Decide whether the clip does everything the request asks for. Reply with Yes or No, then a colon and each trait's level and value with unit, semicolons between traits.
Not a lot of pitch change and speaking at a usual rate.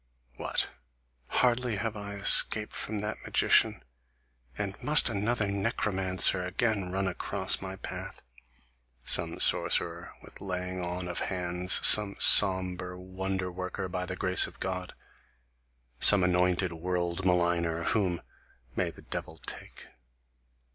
No: narrow, 1.9 semitones; slow, 120 wpm